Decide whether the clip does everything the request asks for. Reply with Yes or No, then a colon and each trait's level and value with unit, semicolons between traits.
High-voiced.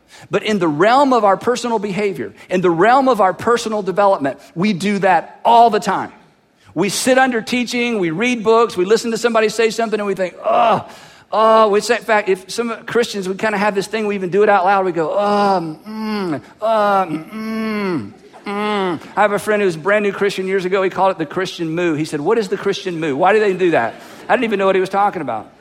Yes: high, 205 Hz